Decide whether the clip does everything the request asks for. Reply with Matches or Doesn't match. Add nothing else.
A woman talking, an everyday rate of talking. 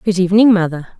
Matches